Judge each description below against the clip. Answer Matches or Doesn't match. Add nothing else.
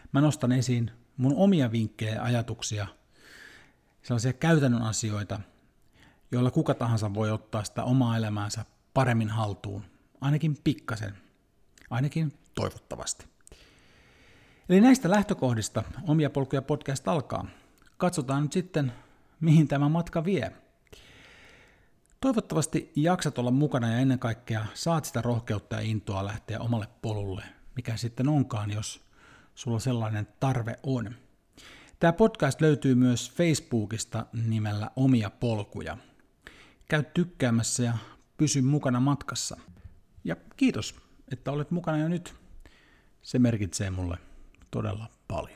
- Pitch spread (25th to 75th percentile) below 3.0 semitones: Doesn't match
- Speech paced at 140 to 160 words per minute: Doesn't match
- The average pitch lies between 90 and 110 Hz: Doesn't match